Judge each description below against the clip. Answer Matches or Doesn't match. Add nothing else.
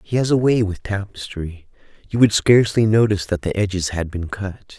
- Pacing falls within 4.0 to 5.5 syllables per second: Matches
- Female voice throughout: Doesn't match